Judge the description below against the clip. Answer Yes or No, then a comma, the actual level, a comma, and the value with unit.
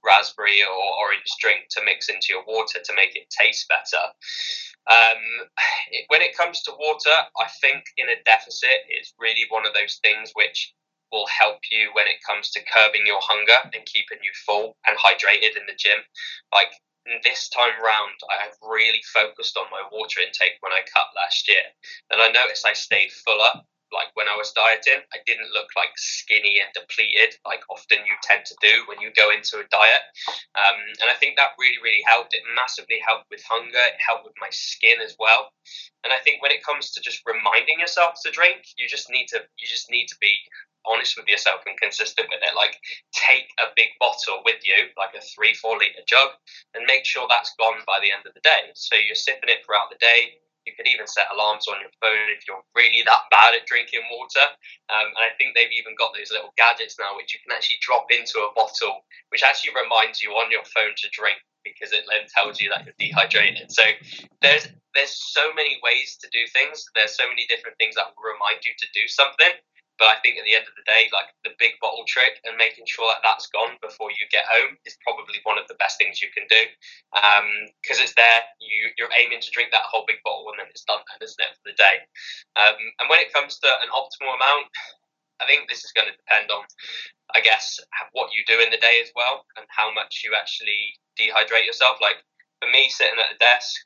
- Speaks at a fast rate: Yes, fast, 220 wpm